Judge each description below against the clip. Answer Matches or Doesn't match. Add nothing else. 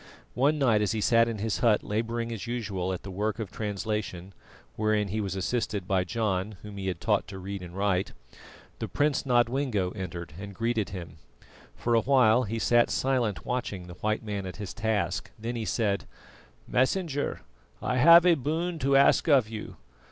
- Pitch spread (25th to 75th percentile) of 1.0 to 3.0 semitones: Doesn't match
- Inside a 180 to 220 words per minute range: Matches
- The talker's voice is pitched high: Doesn't match